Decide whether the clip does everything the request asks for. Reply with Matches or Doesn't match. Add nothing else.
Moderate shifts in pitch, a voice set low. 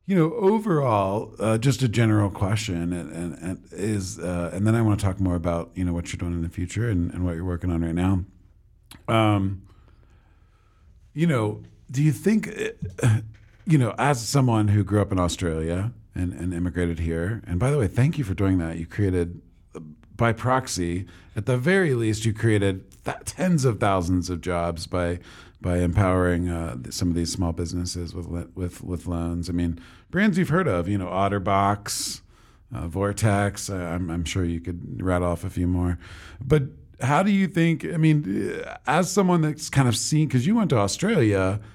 Matches